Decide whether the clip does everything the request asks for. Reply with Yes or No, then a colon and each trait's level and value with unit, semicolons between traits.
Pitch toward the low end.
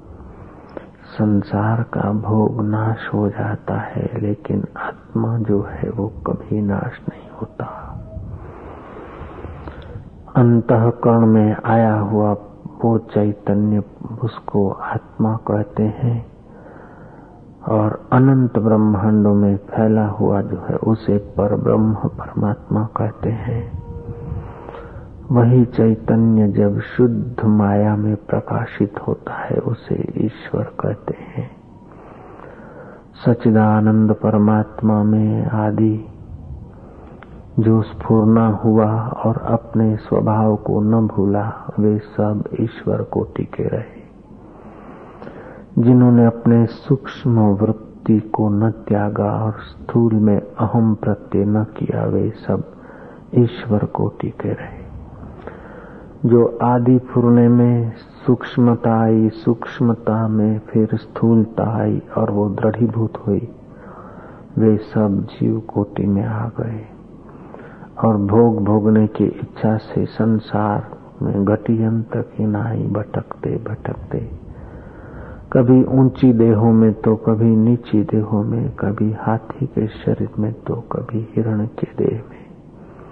Yes: low, 110 Hz